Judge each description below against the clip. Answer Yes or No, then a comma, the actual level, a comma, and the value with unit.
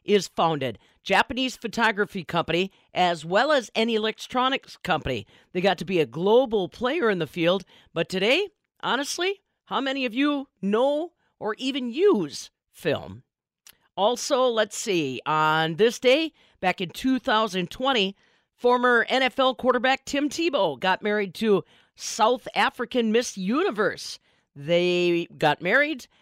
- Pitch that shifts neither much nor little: No, wide, 5.8 semitones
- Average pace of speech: No, slow, 130 wpm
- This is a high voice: Yes, high, 225 Hz